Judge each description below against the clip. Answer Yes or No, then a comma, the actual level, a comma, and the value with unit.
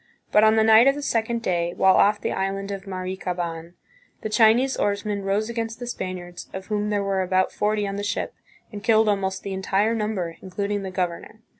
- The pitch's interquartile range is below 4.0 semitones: Yes, narrow, 2.5 semitones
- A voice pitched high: Yes, high, 200 Hz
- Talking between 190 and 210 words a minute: Yes, average, 200 wpm